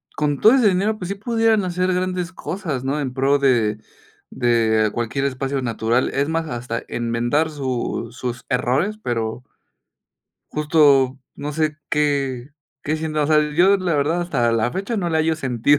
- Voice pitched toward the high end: No, medium, 145 Hz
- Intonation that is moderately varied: No, wide, 5.8 semitones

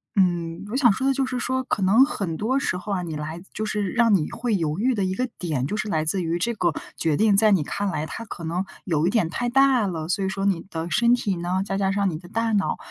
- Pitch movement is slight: No, average, 5.0 semitones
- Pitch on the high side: Yes, high, 195 Hz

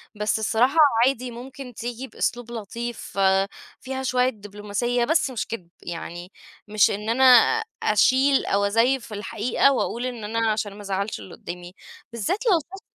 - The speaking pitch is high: Yes, high, 230 Hz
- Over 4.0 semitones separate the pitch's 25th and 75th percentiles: No, average, 3.7 semitones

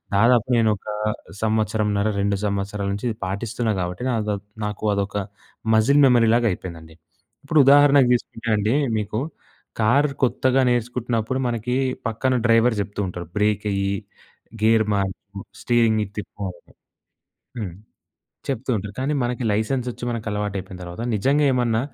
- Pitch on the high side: No, low, 110 Hz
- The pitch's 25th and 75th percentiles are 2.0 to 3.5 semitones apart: Yes, average, 3.2 semitones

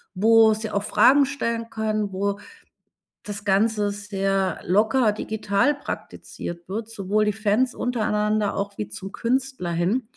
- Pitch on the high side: Yes, high, 210 Hz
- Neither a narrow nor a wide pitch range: No, narrow, 2.3 semitones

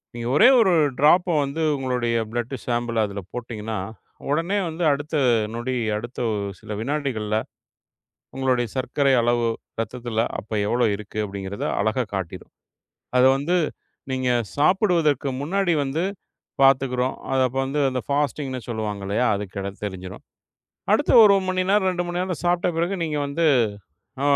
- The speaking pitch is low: Yes, low, 130 Hz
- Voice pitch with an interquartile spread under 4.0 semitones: No, average, 5.2 semitones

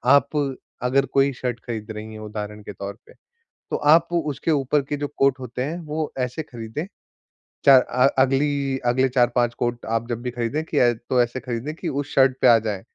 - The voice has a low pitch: Yes, low, 130 Hz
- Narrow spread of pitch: No, average, 3.1 semitones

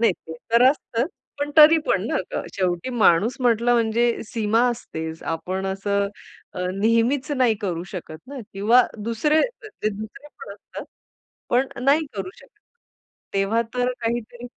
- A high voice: Yes, high, 230 Hz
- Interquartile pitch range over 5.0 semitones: No, average, 4.1 semitones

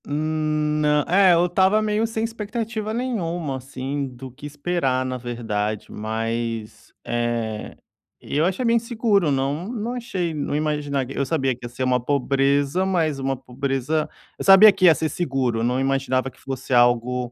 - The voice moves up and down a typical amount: No, wide, 5.7 semitones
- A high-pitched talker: No, medium, 145 Hz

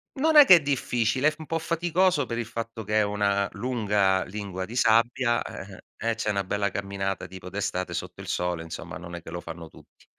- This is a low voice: Yes, low, 105 Hz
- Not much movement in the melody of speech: No, average, 4.8 semitones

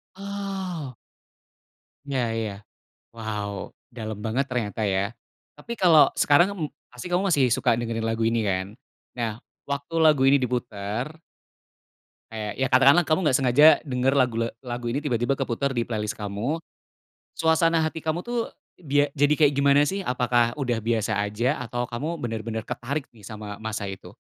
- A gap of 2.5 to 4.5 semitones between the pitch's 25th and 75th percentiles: No, average, 4.9 semitones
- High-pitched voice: No, low, 125 Hz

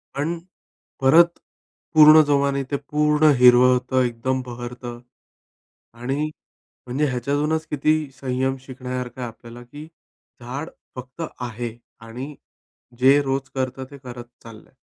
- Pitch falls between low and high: No, low, 130 Hz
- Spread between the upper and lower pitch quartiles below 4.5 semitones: Yes, average, 2.8 semitones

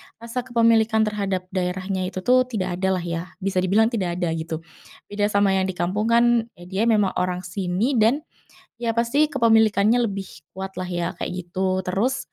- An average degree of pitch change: Yes, average, 3.8 semitones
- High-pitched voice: Yes, high, 195 Hz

